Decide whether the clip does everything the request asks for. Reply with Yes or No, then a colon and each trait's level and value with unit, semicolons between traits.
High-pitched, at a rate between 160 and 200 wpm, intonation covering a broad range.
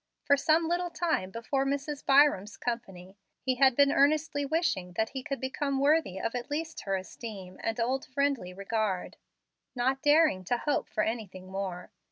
Yes: very high, 255 Hz; average, 170 wpm; wide, 6.4 semitones